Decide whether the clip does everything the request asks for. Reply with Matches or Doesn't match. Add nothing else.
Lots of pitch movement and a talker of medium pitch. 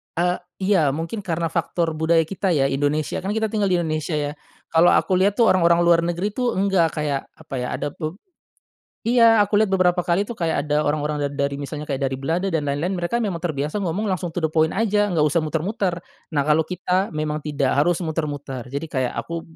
Doesn't match